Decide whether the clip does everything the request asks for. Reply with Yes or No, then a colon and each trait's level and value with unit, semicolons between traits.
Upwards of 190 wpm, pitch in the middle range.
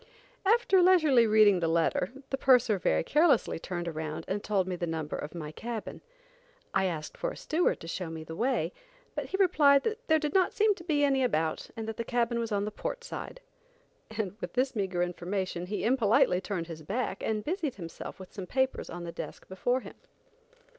No: average, 200 wpm; high, 215 Hz